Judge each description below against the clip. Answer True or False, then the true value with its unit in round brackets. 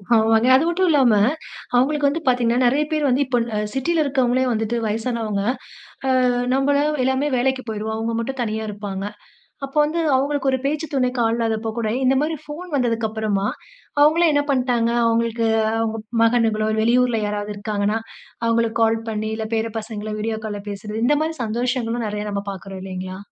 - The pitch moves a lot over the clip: False (3.6 semitones)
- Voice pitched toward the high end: True (230 Hz)